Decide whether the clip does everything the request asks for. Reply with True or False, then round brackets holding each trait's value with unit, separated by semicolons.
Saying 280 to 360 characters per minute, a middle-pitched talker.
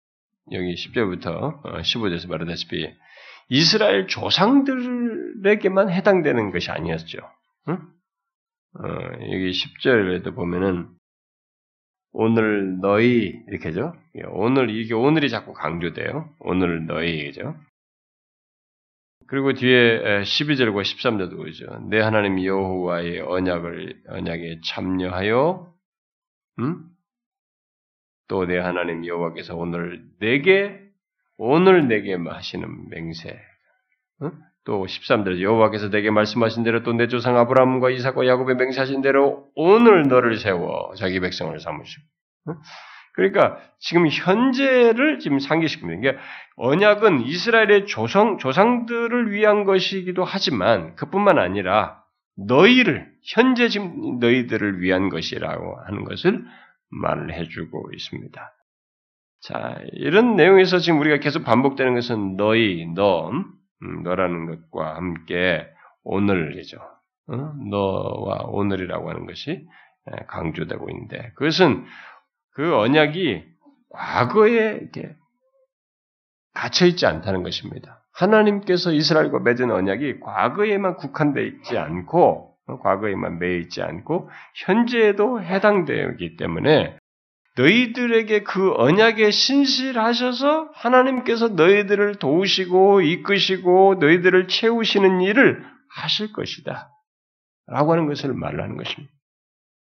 False (265 characters per minute; 150 Hz)